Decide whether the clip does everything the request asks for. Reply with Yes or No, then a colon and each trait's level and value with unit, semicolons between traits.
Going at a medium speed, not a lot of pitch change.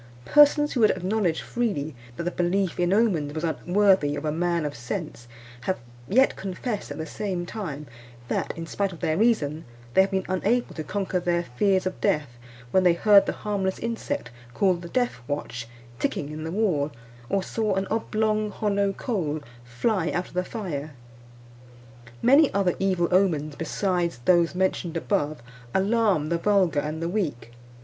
No: average, 170 wpm; average, 4.4 semitones